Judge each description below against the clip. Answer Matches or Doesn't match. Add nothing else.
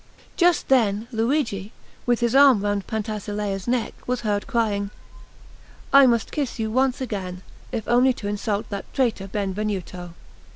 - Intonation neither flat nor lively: Matches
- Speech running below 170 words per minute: Matches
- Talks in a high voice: Matches